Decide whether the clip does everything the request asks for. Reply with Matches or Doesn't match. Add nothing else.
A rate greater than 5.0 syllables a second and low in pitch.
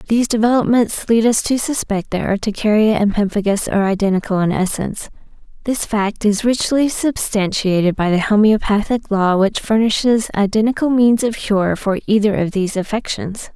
Doesn't match